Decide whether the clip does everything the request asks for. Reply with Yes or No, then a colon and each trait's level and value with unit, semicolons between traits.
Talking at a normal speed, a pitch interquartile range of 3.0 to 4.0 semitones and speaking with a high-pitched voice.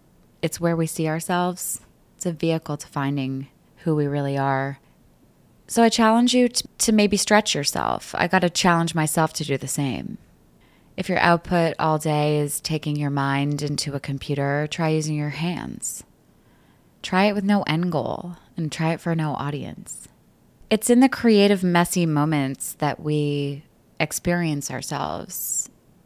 No: average, 160 wpm; average, 3.5 semitones; medium, 155 Hz